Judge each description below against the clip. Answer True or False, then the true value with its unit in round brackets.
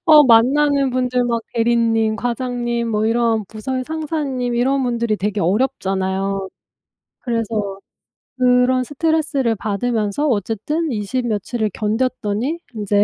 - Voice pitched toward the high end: True (235 Hz)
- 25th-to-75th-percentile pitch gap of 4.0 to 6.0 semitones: False (3.2 semitones)